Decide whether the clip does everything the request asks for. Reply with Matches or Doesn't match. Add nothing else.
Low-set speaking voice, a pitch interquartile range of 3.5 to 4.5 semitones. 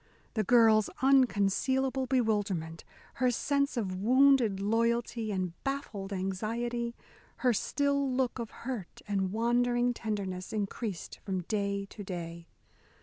Doesn't match